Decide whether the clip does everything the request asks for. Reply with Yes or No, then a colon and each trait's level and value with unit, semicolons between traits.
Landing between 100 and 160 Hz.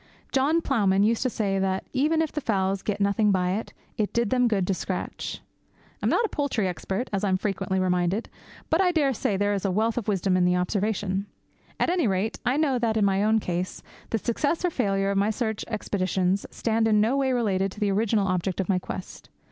No: high, 205 Hz